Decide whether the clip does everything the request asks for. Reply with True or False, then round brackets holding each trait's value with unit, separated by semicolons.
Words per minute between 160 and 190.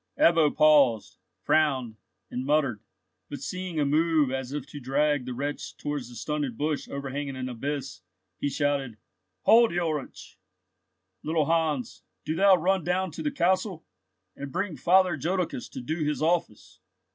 False (150 wpm)